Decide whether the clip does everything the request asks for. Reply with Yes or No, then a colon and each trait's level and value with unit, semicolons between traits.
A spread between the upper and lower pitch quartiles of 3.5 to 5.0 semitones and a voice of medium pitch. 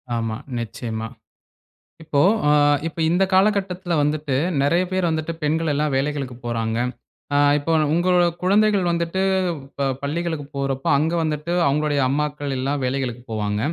Yes: average, 4.1 semitones; medium, 150 Hz